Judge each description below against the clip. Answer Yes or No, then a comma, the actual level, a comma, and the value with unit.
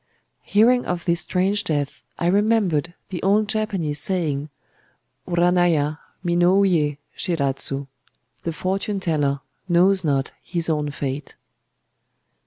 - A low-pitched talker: No, medium, 170 Hz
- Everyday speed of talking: No, slow, 100 wpm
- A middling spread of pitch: Yes, average, 4.5 semitones